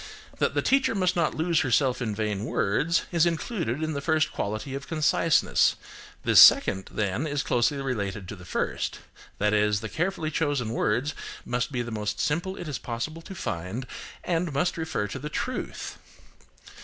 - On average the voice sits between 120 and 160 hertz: Yes, medium, 140 Hz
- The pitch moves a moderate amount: No, wide, 7.0 semitones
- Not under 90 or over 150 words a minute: No, average, 175 wpm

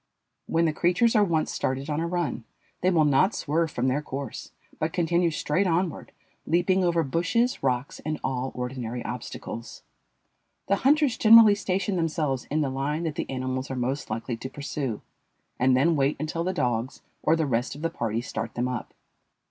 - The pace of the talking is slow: No, average, 180 wpm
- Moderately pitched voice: Yes, medium, 150 Hz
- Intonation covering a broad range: No, average, 4.9 semitones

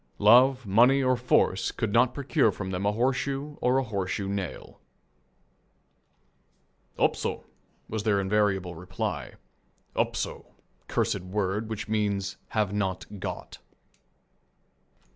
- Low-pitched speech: Yes, low, 105 Hz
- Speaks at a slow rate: Yes, slow, 110 wpm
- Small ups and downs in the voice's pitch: No, average, 4.3 semitones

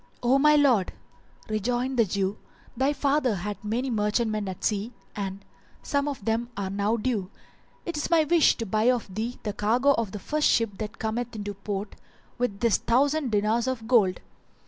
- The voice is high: Yes, high, 225 Hz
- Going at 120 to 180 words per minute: No, average, 190 wpm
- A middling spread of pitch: Yes, average, 3.7 semitones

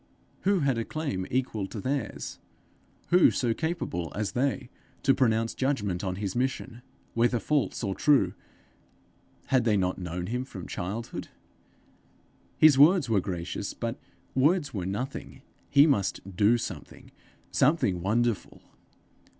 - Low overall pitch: Yes, low, 115 Hz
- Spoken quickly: No, slow, 135 wpm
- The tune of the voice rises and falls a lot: Yes, wide, 5.9 semitones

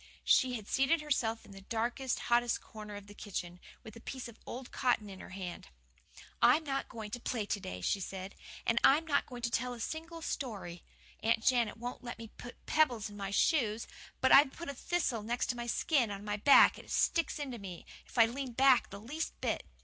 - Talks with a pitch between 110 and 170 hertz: No, high, 235 Hz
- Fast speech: Yes, fast, 220 wpm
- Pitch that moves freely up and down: No, average, 4.3 semitones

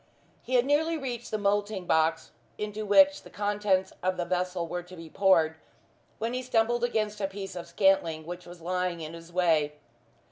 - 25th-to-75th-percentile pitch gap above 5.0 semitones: No, average, 3.9 semitones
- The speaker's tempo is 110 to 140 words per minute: No, average, 185 wpm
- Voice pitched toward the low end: No, high, 190 Hz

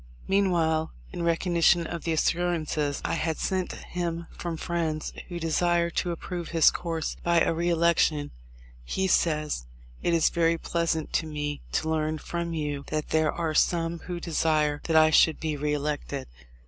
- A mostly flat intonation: Yes, narrow, 1.7 semitones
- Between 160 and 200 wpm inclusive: Yes, average, 165 wpm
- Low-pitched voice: No, medium, 165 Hz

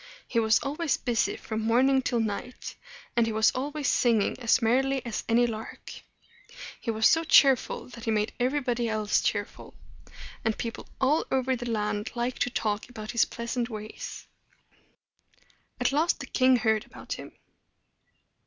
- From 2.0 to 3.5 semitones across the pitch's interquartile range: Yes, average, 2.9 semitones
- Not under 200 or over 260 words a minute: No, average, 155 wpm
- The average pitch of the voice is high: Yes, high, 235 Hz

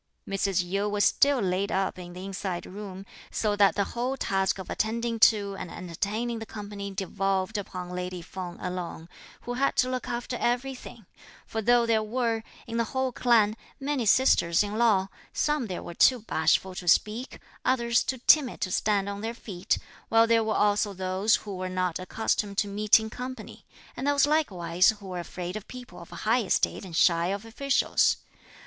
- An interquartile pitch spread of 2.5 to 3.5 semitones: No, average, 4.1 semitones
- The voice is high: Yes, high, 205 Hz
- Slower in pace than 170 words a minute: No, average, 180 wpm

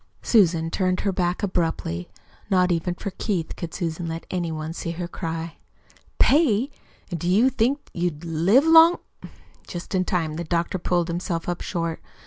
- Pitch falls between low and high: Yes, medium, 175 Hz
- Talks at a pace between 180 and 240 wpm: No, average, 170 wpm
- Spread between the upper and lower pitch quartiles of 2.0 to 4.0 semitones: Yes, narrow, 2.6 semitones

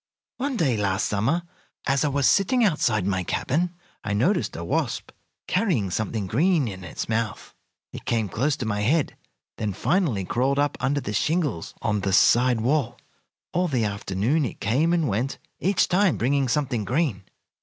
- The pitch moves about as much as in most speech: No, wide, 7.2 semitones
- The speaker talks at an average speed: Yes, average, 170 wpm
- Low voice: Yes, low, 125 Hz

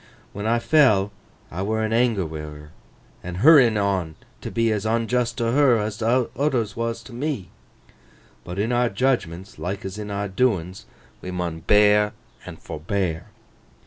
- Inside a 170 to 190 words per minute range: No, average, 160 wpm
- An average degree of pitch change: Yes, average, 4.0 semitones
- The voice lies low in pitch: Yes, low, 105 Hz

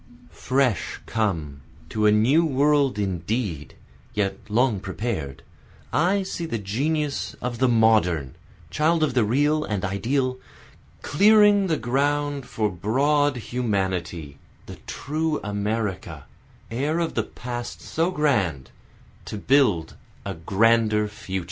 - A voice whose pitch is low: Yes, low, 115 Hz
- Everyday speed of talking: No, slow, 120 wpm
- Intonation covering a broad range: Yes, wide, 6.4 semitones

